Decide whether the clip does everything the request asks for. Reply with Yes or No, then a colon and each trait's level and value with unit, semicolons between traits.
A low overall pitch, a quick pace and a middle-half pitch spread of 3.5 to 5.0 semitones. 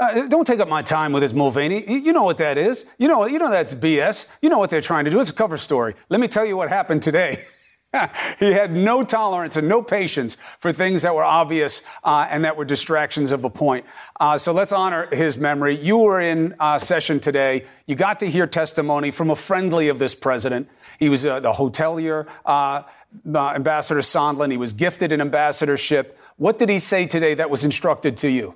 No: medium, 155 Hz; fast, 220 wpm; average, 4.5 semitones